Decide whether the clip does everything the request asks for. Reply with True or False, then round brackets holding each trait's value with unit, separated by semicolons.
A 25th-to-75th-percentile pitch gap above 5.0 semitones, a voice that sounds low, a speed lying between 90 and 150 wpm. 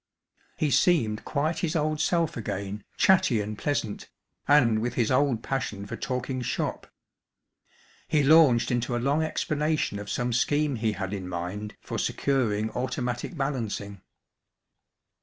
True (5.6 semitones; 125 Hz; 140 wpm)